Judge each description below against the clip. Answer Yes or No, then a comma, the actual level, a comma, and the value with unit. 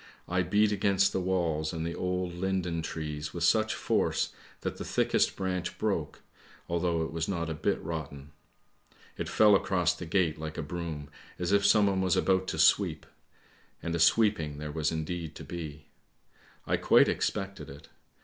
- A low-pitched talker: Yes, very low, 85 Hz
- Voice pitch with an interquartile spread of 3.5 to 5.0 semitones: No, average, 3.0 semitones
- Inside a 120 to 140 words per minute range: No, average, 170 wpm